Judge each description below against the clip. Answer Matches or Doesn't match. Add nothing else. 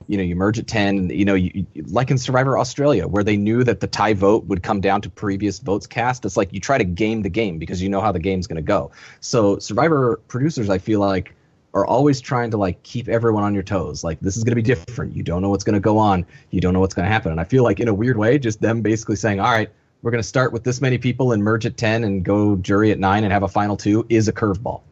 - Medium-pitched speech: Doesn't match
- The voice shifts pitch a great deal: Doesn't match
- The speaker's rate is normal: Doesn't match